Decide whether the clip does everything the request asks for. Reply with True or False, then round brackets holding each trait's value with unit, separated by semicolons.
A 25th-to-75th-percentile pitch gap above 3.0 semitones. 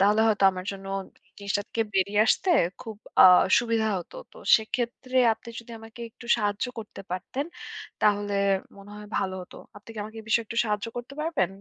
False (2.5 semitones)